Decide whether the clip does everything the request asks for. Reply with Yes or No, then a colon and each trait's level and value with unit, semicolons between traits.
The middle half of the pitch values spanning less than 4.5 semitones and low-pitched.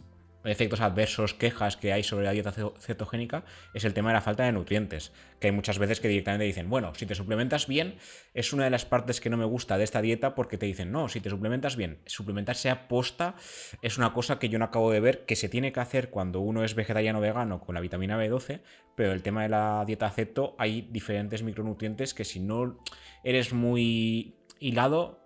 Yes: average, 2.9 semitones; low, 110 Hz